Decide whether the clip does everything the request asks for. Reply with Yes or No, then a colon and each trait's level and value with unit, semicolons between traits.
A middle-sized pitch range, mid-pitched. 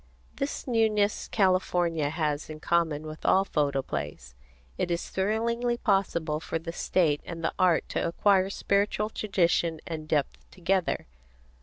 Yes: average, 4.2 semitones; medium, 170 Hz